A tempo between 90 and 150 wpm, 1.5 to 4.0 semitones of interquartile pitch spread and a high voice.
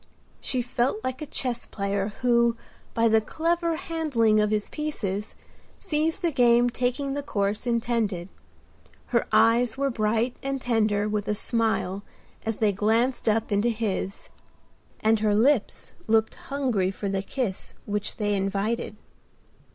Yes: average, 145 wpm; average, 3.4 semitones; high, 230 Hz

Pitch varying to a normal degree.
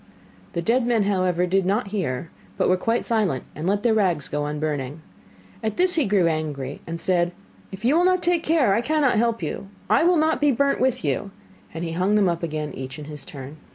No: wide, 7.2 semitones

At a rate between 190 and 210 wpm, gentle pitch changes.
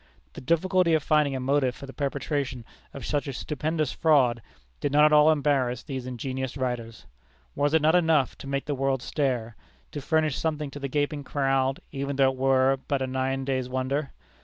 Yes: average, 195 wpm; narrow, 2.3 semitones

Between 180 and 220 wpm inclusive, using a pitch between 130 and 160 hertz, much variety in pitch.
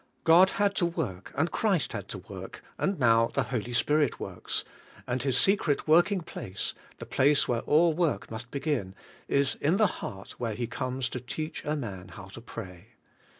Yes: average, 190 wpm; low, 135 Hz; wide, 5.9 semitones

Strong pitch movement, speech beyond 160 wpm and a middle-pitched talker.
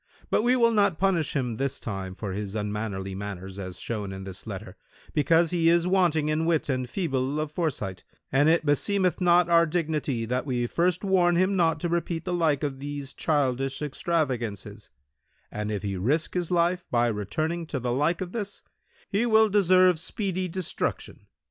Yes: wide, 6.6 semitones; average, 180 wpm; medium, 155 Hz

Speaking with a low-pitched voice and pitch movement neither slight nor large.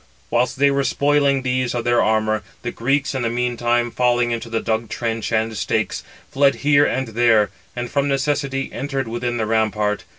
Yes: low, 120 Hz; average, 3.1 semitones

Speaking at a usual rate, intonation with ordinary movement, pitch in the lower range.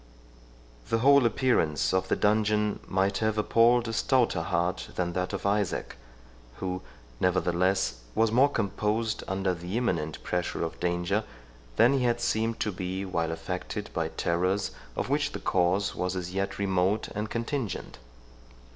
Yes: average, 150 wpm; average, 3.8 semitones; very low, 95 Hz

